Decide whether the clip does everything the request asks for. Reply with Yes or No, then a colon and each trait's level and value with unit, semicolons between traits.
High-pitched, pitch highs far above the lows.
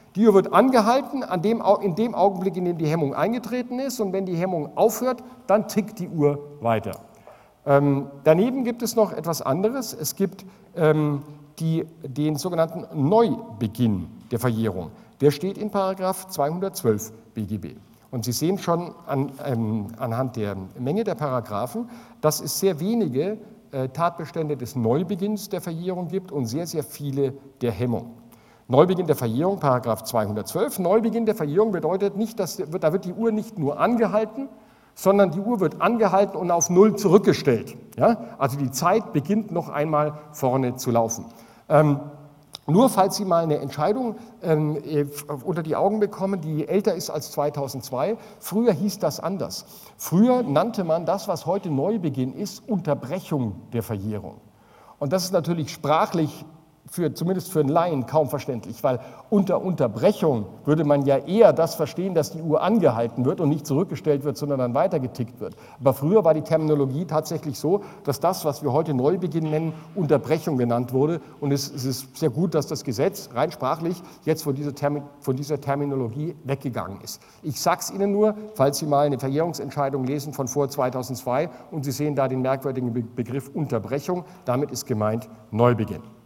No: medium, 155 Hz; wide, 5.9 semitones